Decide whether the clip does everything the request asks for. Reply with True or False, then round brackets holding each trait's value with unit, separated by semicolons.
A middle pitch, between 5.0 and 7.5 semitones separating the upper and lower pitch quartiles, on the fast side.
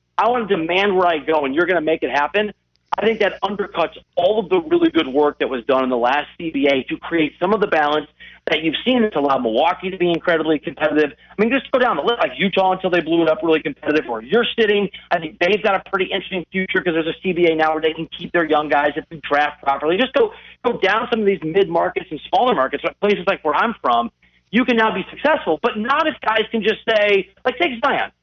True (180 Hz; 5.6 semitones; 260 wpm)